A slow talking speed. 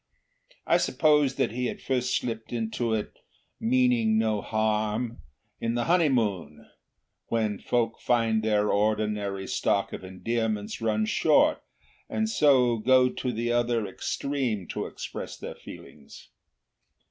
Yes: slow, 125 wpm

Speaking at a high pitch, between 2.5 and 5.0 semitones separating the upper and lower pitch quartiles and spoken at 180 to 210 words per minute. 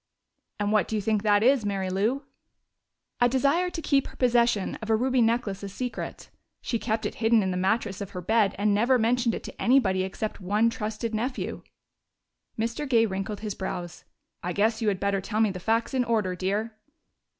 Yes: high, 220 Hz; average, 2.9 semitones; average, 200 wpm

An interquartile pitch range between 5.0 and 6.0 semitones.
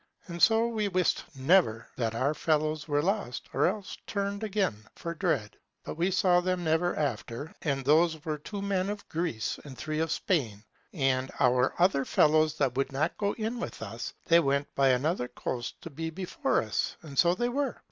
Yes: average, 5.3 semitones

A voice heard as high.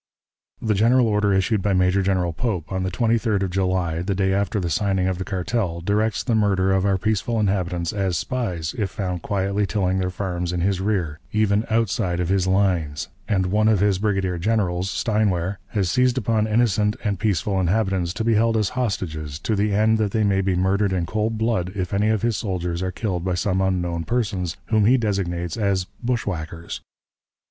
No: very low, 95 Hz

